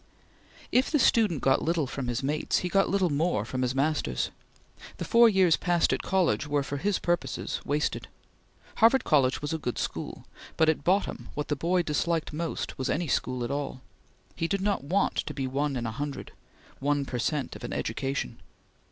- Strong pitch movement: No, average, 4.4 semitones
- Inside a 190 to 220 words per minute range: Yes, average, 195 wpm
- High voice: No, medium, 150 Hz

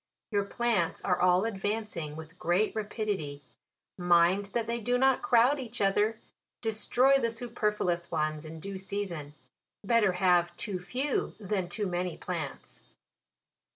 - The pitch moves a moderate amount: Yes, average, 4.4 semitones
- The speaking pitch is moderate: No, high, 195 Hz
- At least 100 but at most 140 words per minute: Yes, slow, 135 wpm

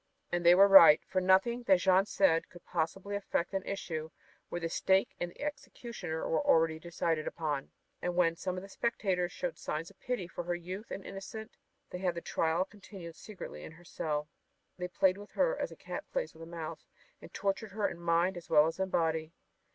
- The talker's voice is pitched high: No, medium, 180 Hz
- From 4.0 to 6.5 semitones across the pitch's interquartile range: No, average, 2.9 semitones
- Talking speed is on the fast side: Yes, fast, 210 wpm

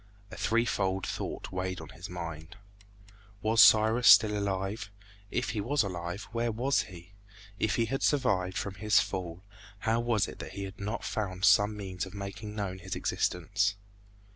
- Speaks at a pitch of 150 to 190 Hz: No, low, 100 Hz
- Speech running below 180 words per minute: Yes, average, 165 wpm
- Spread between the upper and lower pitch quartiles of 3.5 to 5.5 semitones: No, average, 3.0 semitones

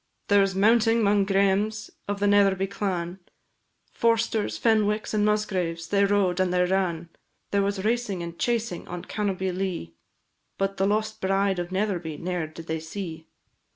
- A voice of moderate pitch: No, high, 195 Hz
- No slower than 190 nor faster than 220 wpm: No, average, 155 wpm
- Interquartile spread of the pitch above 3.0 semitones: No, narrow, 2.6 semitones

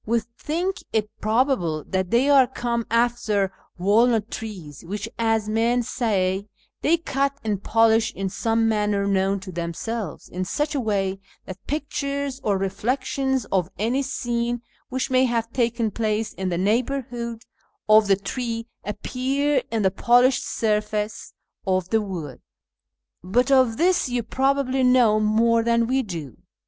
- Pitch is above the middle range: Yes, high, 225 Hz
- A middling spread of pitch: Yes, average, 4.0 semitones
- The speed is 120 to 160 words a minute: Yes, average, 145 wpm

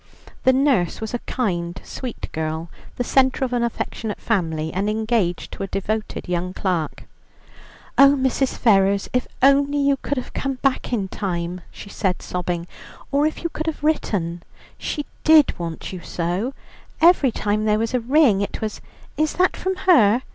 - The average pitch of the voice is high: Yes, high, 220 Hz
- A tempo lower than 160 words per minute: No, average, 170 wpm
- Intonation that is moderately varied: No, wide, 7.0 semitones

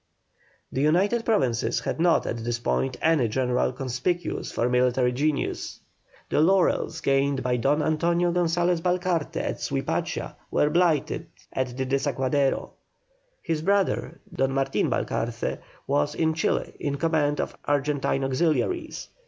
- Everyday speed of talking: No, slow, 130 wpm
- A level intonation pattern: No, average, 4.4 semitones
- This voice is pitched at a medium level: Yes, medium, 145 Hz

